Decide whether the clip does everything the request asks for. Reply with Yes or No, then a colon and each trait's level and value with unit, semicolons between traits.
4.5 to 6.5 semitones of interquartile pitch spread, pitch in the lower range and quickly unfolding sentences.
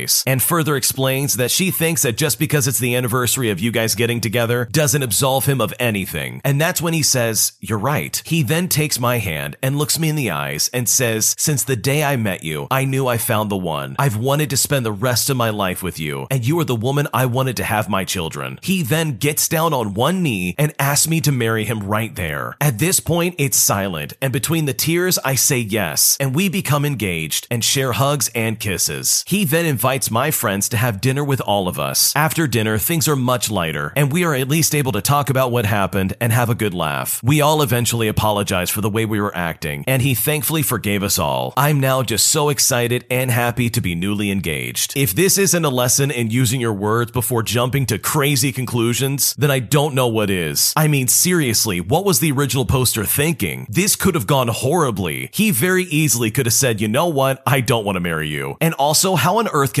Yes: average, 5.2 semitones; low, 130 Hz; fast, 230 wpm